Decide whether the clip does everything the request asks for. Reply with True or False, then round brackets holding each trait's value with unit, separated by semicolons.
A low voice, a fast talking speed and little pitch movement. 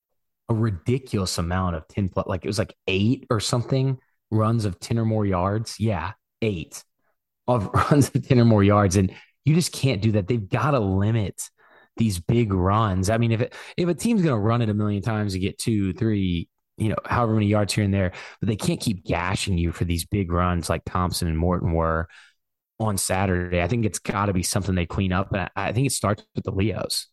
False (105 Hz; 225 wpm; 3.7 semitones)